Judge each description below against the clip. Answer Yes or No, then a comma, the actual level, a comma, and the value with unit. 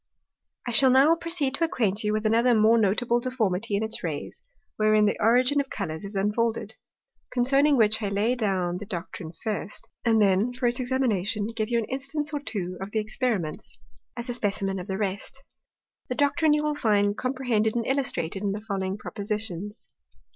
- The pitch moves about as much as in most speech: Yes, average, 3.9 semitones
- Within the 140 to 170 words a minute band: No, average, 185 wpm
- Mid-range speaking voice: No, high, 220 Hz